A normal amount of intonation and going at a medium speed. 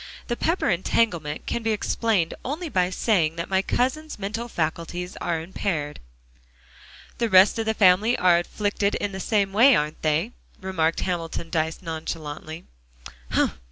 Yes: average, 5.0 semitones; average, 145 wpm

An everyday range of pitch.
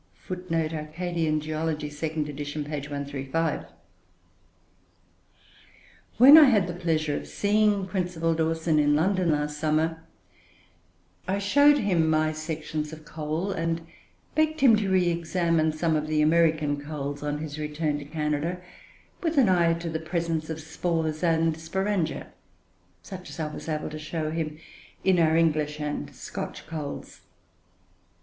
No: narrow, 2.3 semitones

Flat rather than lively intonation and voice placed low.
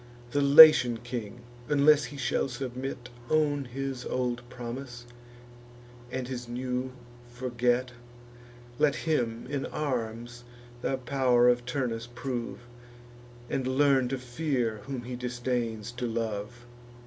Yes: narrow, 1.9 semitones; low, 125 Hz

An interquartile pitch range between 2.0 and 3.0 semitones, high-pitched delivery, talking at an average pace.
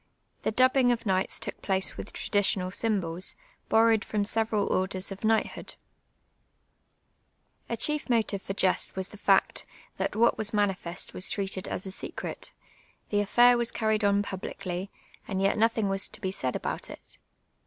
Yes: average, 2.7 semitones; high, 205 Hz; average, 160 wpm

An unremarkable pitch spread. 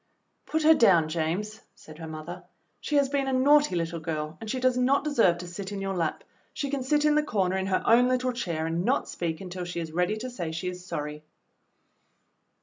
No: wide, 7.3 semitones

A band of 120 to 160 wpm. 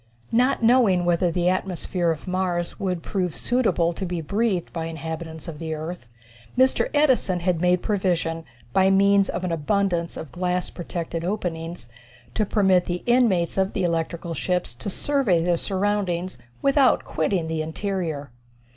Yes: average, 155 wpm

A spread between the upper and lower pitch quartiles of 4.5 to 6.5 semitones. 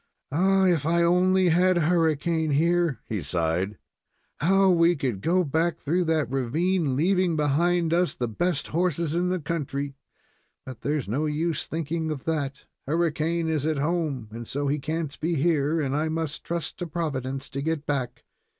No: average, 3.4 semitones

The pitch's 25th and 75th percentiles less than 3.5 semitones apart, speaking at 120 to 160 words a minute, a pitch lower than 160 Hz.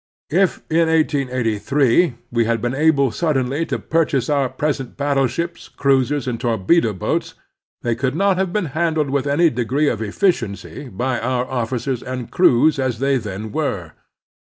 No: average, 4.3 semitones; average, 155 wpm; low, 135 Hz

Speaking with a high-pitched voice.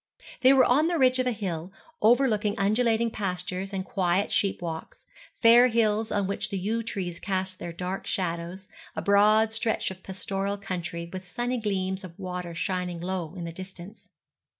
Yes: high, 195 Hz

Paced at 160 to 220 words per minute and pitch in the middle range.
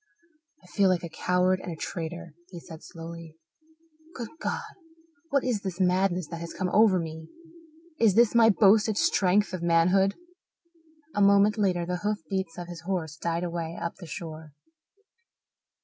Yes: average, 165 wpm; medium, 180 Hz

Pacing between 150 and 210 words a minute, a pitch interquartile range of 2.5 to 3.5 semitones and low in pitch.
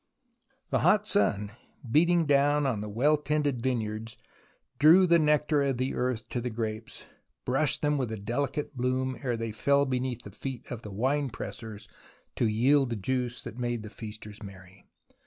No: average, 175 wpm; average, 4.4 semitones; low, 125 Hz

